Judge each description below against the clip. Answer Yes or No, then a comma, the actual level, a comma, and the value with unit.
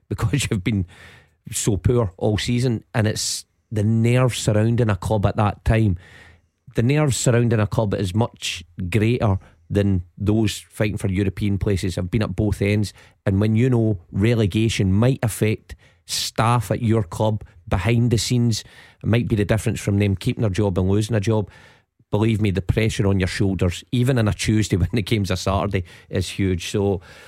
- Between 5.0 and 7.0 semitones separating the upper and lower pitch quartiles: No, average, 2.8 semitones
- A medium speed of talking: Yes, average, 185 wpm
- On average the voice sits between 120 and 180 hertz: No, low, 105 Hz